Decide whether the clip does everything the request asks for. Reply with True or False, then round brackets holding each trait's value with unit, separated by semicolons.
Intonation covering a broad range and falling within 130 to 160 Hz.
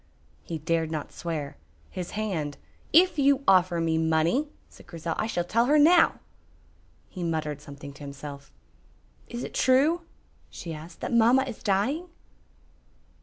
False (8.1 semitones; 175 Hz)